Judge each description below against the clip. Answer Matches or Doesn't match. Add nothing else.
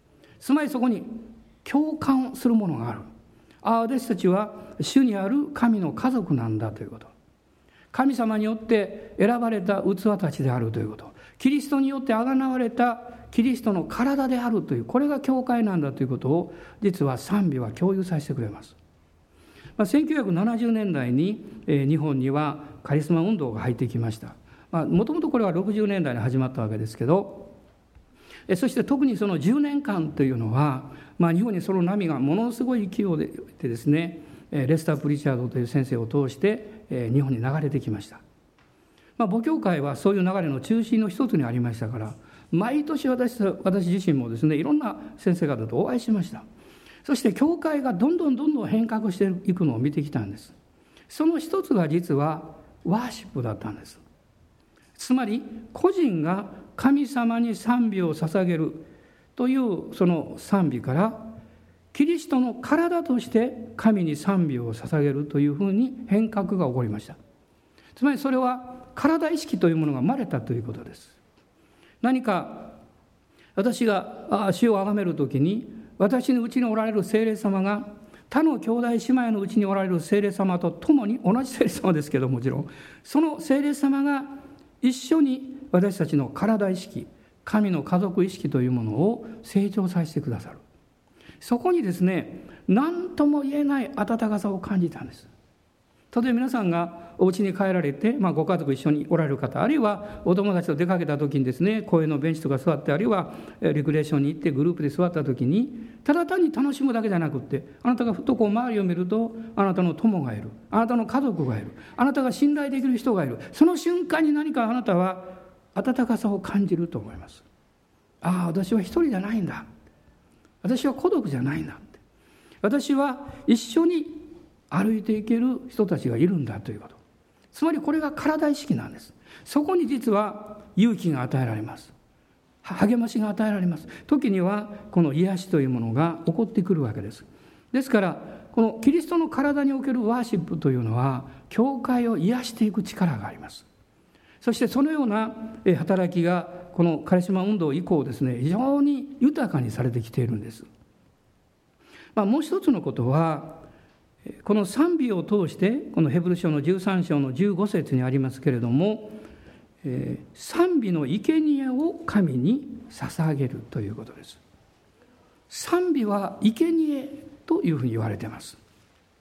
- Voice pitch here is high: Matches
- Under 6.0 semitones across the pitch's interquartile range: Doesn't match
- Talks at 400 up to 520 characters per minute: Doesn't match